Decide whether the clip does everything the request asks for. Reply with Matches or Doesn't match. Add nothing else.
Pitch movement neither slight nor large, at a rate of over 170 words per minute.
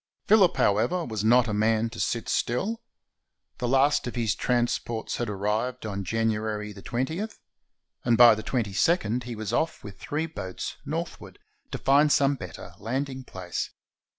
Doesn't match